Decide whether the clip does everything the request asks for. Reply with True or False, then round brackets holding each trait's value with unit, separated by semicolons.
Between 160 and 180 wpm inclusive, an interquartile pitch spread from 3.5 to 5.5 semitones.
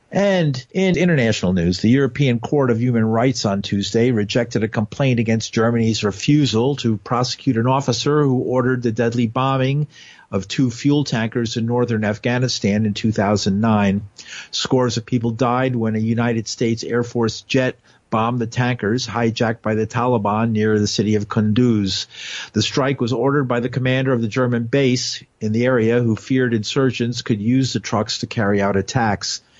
False (170 wpm; 2.7 semitones)